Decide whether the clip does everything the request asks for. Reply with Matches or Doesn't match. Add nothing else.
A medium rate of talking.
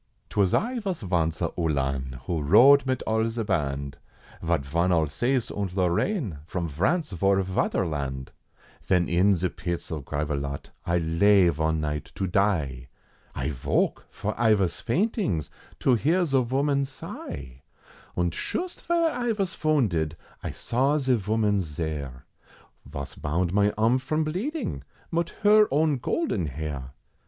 Matches